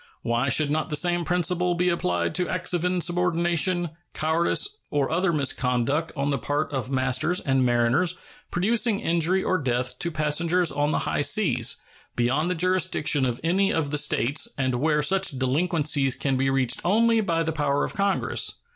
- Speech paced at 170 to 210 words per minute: Yes, average, 175 wpm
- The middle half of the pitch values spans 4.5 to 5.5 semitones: Yes, average, 4.8 semitones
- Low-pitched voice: No, medium, 155 Hz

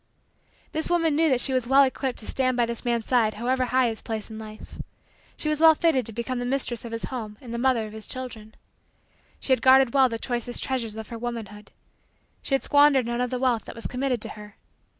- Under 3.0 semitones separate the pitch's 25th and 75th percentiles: Yes, narrow, 2.6 semitones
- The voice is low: No, high, 245 Hz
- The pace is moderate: No, fast, 235 wpm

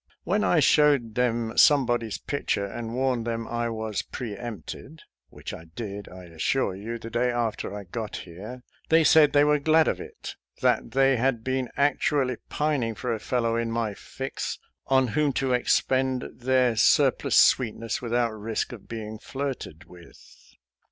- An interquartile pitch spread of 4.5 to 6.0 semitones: No, average, 3.2 semitones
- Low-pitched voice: Yes, low, 120 Hz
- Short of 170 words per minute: No, average, 180 wpm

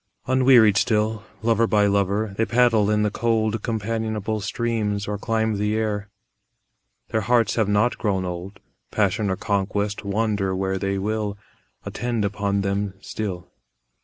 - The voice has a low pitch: Yes, low, 105 Hz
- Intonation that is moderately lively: No, narrow, 1.8 semitones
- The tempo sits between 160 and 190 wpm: No, average, 140 wpm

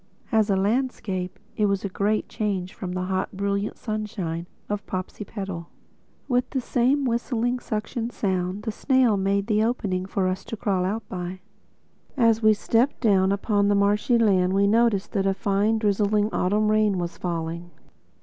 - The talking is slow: No, average, 165 wpm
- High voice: Yes, high, 205 Hz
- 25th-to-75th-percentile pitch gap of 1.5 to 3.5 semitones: Yes, average, 2.7 semitones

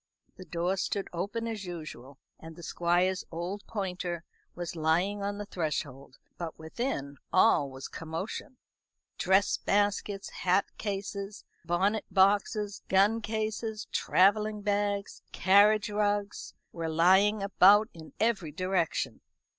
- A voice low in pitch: No, high, 195 Hz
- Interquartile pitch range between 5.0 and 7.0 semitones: No, average, 3.3 semitones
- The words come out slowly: Yes, slow, 120 wpm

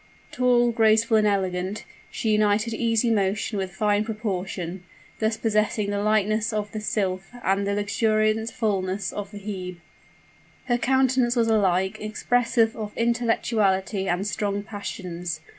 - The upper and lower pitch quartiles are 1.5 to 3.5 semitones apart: Yes, narrow, 2.4 semitones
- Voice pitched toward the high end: Yes, high, 210 Hz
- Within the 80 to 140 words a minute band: Yes, slow, 135 wpm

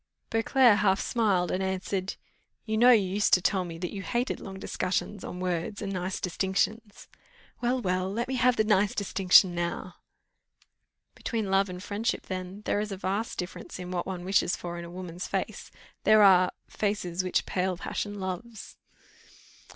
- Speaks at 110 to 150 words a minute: No, average, 175 wpm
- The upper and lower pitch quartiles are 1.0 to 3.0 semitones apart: Yes, narrow, 2.6 semitones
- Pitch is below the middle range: No, high, 190 Hz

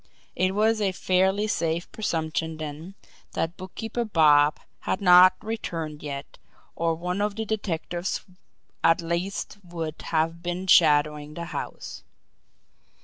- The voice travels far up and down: No, average, 3.3 semitones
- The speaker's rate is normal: No, slow, 125 wpm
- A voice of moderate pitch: Yes, medium, 175 Hz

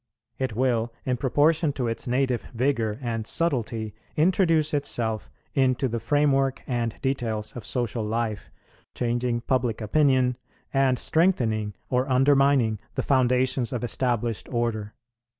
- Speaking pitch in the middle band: No, low, 125 Hz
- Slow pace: Yes, slow, 125 wpm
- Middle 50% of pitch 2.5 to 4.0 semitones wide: Yes, average, 3.0 semitones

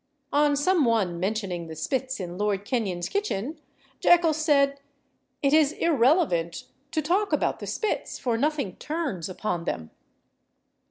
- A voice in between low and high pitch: No, very high, 265 Hz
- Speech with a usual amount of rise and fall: No, wide, 8.4 semitones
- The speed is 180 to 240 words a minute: No, average, 140 wpm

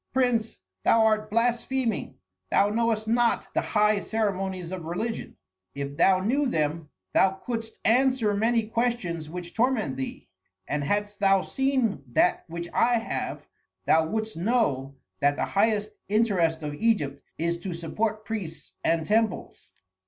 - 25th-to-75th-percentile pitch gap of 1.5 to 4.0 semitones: No, average, 5.2 semitones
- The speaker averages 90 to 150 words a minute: Yes, average, 140 wpm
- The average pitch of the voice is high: Yes, high, 210 Hz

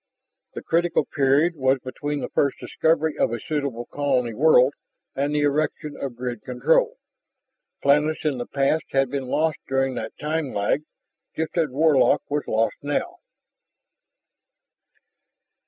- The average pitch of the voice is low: No, medium, 145 Hz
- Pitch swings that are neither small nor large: Yes, average, 3.1 semitones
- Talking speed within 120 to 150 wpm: Yes, average, 140 wpm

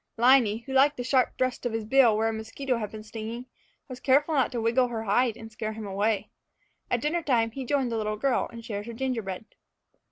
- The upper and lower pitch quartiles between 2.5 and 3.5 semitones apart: Yes, average, 2.8 semitones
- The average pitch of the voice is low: No, high, 235 Hz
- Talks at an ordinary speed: No, fast, 225 wpm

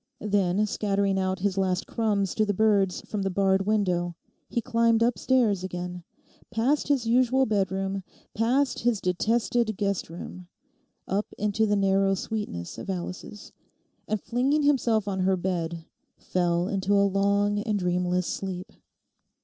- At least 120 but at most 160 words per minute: Yes, average, 140 wpm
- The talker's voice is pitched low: No, high, 200 Hz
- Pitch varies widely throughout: No, average, 2.9 semitones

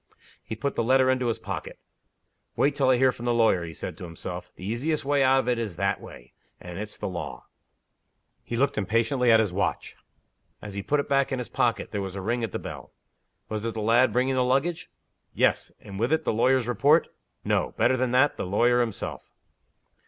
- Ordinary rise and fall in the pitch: Yes, average, 4.0 semitones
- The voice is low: Yes, low, 120 Hz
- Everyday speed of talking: No, fast, 220 wpm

